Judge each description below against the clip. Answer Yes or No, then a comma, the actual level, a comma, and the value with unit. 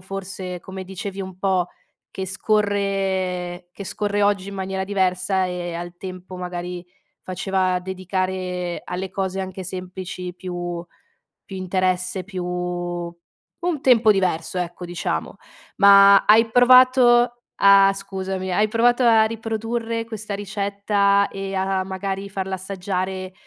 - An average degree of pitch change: No, narrow, 1.7 semitones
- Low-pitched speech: No, high, 190 Hz